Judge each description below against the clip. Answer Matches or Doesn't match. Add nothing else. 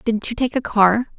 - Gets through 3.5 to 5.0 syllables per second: Matches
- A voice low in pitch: Doesn't match